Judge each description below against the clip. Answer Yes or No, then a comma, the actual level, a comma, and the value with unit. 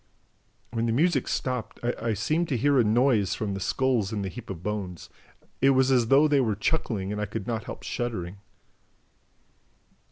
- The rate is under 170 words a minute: No, average, 185 wpm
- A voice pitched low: Yes, low, 115 Hz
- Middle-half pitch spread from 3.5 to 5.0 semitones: Yes, average, 4.4 semitones